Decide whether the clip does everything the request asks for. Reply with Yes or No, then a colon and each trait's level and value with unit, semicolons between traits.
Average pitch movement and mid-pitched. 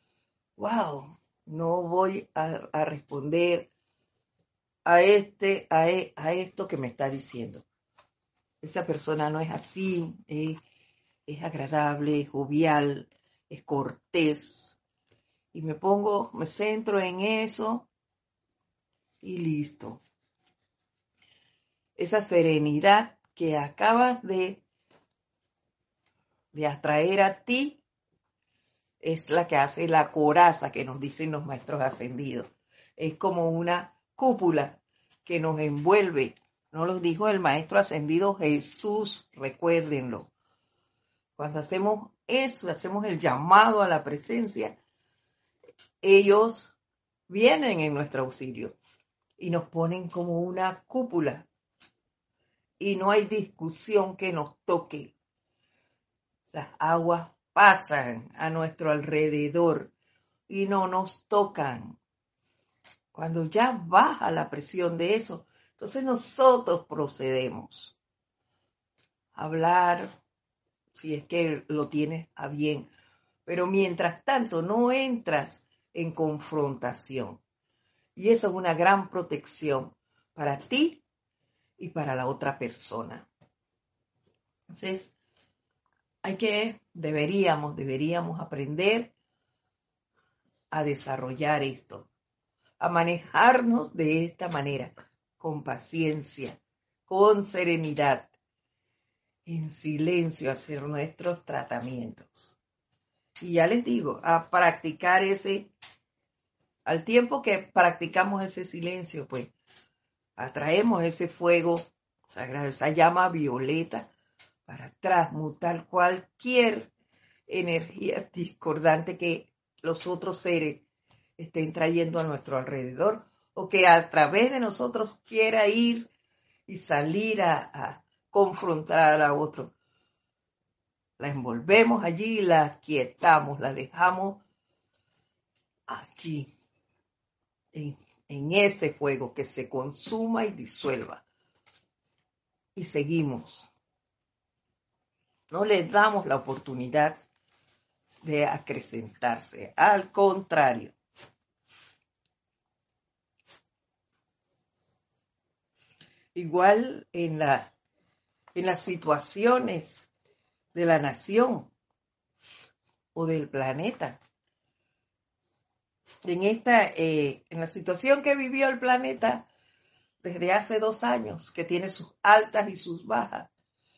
Yes: average, 4.9 semitones; medium, 165 Hz